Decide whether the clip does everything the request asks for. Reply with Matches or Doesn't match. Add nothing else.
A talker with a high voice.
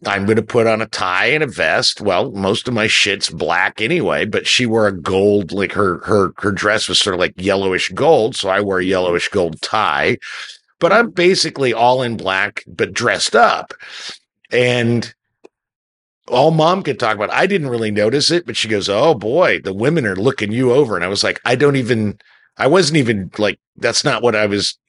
Doesn't match